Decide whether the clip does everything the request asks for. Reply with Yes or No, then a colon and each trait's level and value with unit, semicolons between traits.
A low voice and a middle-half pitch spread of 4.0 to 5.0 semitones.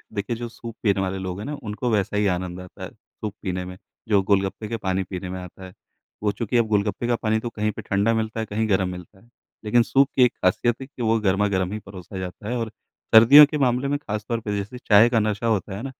No: low, 105 Hz; average, 3.4 semitones